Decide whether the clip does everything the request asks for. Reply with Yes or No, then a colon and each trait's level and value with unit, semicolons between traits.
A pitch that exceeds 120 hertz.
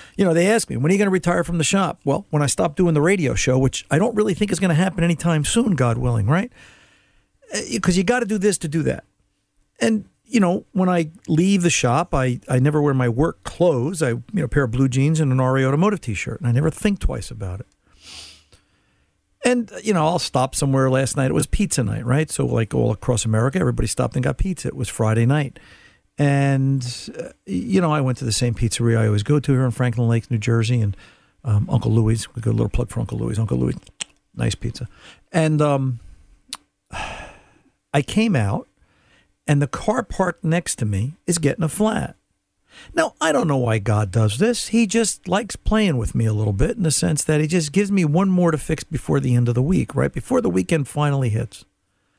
Yes: medium, 140 Hz